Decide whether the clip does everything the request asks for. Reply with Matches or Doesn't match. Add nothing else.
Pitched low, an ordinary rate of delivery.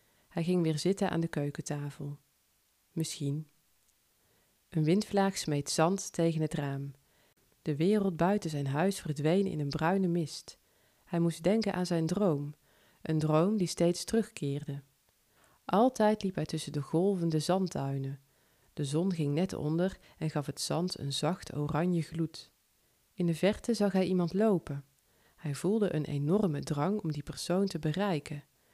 Doesn't match